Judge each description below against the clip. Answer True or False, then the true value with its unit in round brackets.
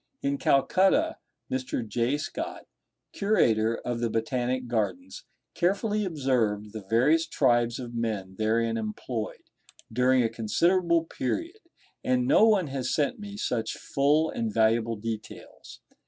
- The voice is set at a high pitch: False (125 Hz)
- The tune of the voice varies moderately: False (6.4 semitones)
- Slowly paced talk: True (125 wpm)